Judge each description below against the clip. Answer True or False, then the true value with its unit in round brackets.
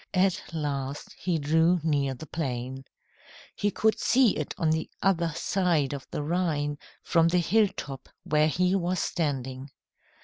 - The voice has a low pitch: False (160 Hz)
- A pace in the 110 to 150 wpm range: True (145 wpm)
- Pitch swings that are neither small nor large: True (4.1 semitones)